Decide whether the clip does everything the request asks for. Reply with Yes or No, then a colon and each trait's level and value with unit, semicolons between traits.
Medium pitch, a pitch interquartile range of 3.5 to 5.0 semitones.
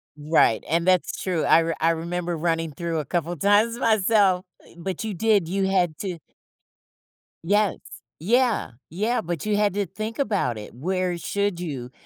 Yes: medium, 180 Hz; average, 3.8 semitones